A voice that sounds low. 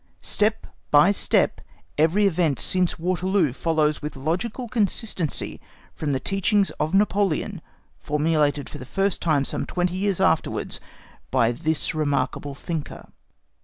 No: medium, 165 Hz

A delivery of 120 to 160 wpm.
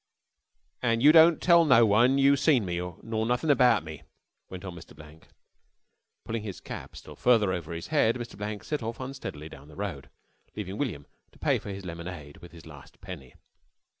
No: average, 190 wpm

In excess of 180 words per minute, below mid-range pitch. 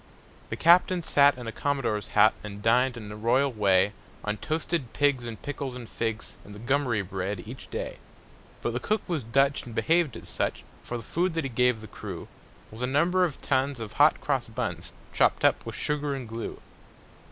Yes: average, 195 wpm; low, 125 Hz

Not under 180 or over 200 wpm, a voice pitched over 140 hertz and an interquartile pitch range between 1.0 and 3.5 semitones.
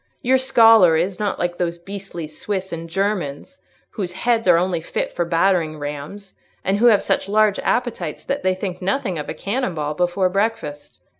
No: average, 190 wpm; medium, 185 Hz; average, 3.9 semitones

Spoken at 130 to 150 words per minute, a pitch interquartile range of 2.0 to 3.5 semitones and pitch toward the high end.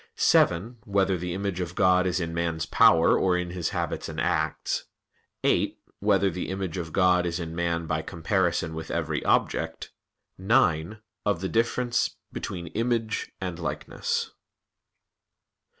No: average, 145 wpm; average, 2.7 semitones; very low, 90 Hz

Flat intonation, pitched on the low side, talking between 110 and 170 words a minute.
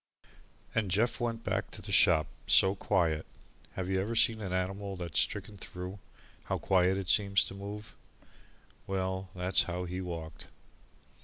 Yes: narrow, 1.9 semitones; very low, 95 Hz; average, 160 wpm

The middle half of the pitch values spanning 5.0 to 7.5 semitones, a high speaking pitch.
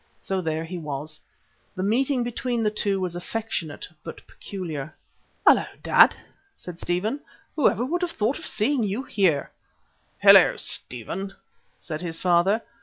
Yes: wide, 5.6 semitones; high, 195 Hz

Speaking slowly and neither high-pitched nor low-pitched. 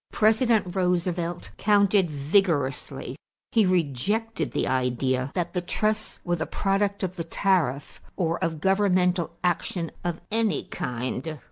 Yes: slow, 125 wpm; medium, 180 Hz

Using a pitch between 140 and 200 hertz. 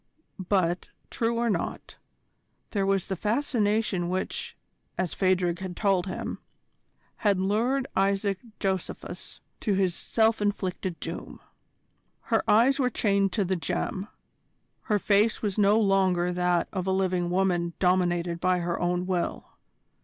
Yes: high, 190 Hz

